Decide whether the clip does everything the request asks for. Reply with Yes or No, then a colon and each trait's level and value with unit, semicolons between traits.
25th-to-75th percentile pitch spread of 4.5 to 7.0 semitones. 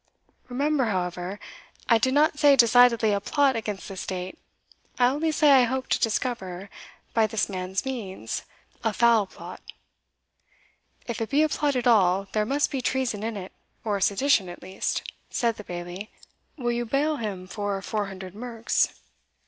Yes: average, 5.0 semitones